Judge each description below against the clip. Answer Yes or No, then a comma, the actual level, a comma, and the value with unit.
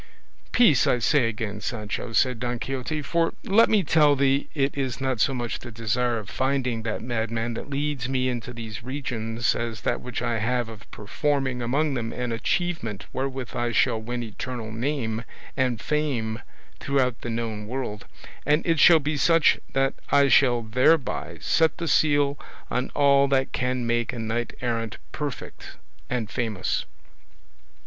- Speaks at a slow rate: No, average, 165 wpm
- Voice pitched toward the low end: Yes, low, 125 Hz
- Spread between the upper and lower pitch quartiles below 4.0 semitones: Yes, average, 3.4 semitones